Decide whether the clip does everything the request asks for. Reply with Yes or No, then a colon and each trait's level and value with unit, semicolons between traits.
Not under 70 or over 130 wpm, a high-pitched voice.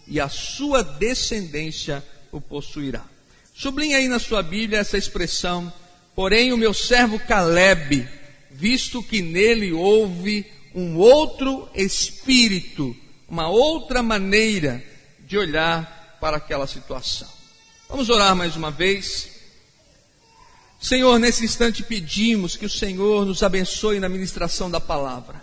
Yes: slow, 120 wpm; high, 195 Hz